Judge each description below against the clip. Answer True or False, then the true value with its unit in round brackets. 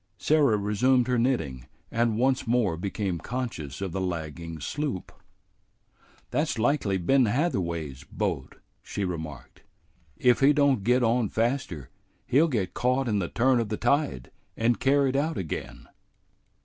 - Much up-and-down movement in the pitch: True (6.5 semitones)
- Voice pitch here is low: True (115 Hz)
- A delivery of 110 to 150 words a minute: True (140 wpm)